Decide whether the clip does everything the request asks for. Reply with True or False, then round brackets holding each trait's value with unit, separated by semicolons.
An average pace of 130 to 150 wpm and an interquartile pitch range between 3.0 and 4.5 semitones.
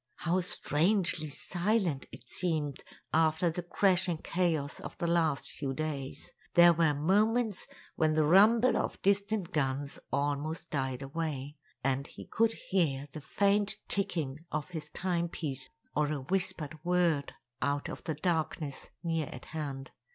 True (140 wpm; 3.8 semitones)